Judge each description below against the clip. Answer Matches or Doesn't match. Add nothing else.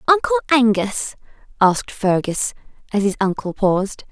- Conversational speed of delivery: Doesn't match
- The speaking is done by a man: Doesn't match